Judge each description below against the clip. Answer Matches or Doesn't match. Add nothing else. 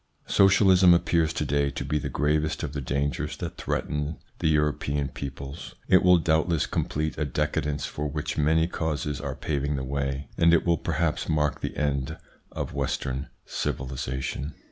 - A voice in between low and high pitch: Doesn't match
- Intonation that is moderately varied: Doesn't match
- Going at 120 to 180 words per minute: Matches